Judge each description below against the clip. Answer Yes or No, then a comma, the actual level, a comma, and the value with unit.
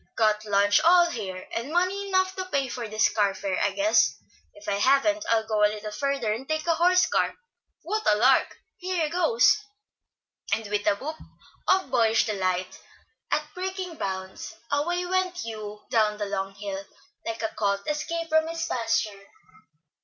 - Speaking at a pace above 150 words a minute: Yes, average, 170 wpm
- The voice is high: Yes, high, 235 Hz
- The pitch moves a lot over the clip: Yes, wide, 8.0 semitones